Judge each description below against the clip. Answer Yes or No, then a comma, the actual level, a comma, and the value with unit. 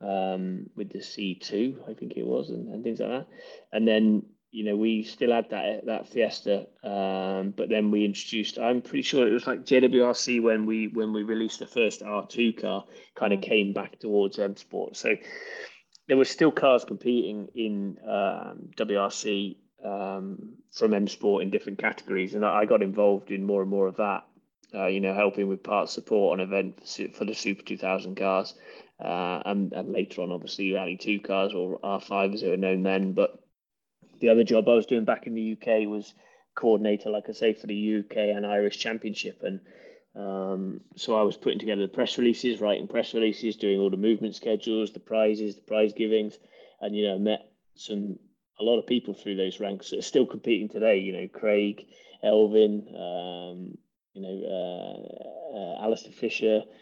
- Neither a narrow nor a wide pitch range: No, narrow, 2.0 semitones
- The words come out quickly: No, average, 195 wpm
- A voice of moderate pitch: No, low, 105 Hz